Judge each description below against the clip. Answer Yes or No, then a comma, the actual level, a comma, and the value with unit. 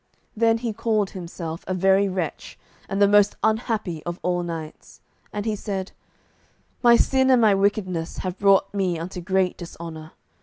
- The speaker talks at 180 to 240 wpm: No, average, 160 wpm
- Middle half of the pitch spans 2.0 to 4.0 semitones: Yes, average, 3.4 semitones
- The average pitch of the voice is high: Yes, high, 195 Hz